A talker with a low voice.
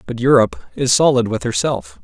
Yes: low, 130 Hz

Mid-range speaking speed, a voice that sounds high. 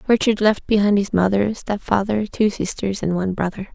Yes: average, 190 wpm; high, 200 Hz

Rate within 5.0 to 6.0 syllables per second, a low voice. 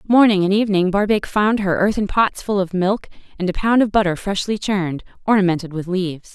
No: 5.8 syllables/s; high, 195 Hz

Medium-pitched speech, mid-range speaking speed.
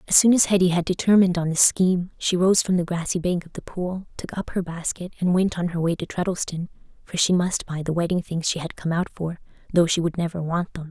No: medium, 175 Hz; fast, 260 wpm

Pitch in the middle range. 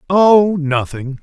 Yes: medium, 165 Hz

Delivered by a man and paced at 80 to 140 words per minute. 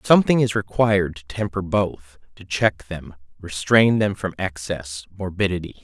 Yes: male; slow, 135 wpm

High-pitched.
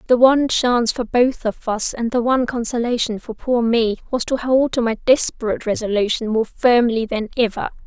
Yes: high, 235 Hz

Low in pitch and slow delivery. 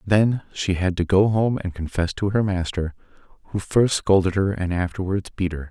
No: very low, 95 Hz; average, 200 wpm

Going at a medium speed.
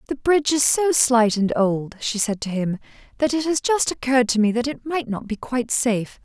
No: fast, 240 wpm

